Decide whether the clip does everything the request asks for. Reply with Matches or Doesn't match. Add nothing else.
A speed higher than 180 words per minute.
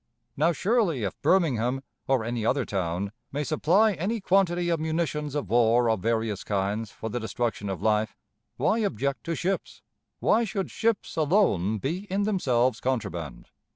Doesn't match